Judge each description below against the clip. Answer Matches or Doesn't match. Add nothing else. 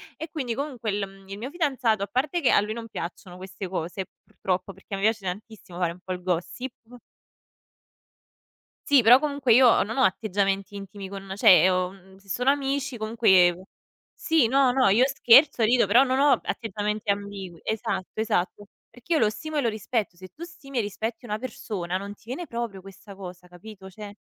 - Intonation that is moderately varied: Matches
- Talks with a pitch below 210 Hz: Doesn't match